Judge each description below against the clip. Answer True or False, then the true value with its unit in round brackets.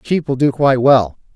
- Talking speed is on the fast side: True (220 wpm)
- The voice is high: False (135 Hz)